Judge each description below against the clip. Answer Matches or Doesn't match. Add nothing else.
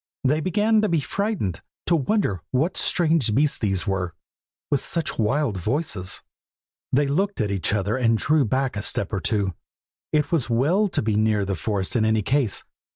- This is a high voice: Doesn't match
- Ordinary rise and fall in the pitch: Doesn't match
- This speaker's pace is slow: Doesn't match